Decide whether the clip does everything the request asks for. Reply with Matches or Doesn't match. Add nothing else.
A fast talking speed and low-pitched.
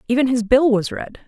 Doesn't match